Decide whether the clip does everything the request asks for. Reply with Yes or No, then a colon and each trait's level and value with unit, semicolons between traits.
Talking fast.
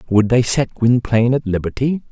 No: average, 170 wpm